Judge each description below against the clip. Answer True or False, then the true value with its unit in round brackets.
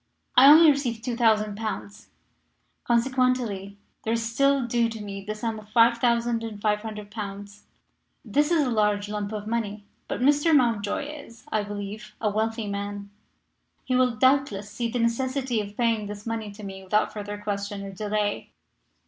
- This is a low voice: False (220 Hz)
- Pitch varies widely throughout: False (2.7 semitones)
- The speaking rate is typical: True (155 wpm)